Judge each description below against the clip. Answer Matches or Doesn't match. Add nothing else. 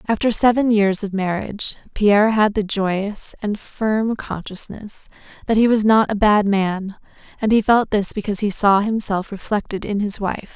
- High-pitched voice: Matches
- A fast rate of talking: Doesn't match